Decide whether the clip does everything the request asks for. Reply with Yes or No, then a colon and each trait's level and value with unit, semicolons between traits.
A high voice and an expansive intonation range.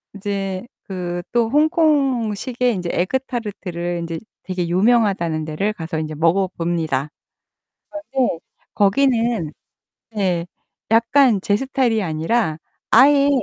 Yes: high, 200 Hz; wide, 5.9 semitones